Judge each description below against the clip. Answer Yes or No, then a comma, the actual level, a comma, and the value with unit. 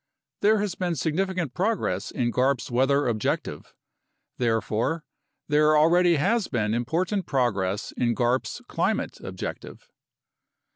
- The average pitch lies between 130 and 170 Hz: Yes, medium, 140 Hz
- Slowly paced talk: Yes, slow, 115 wpm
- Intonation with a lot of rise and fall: Yes, wide, 6.7 semitones